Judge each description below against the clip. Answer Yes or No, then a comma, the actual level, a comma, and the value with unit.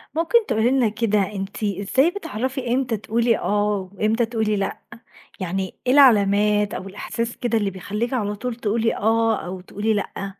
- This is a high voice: Yes, high, 215 Hz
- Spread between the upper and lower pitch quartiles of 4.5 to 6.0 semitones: No, average, 2.7 semitones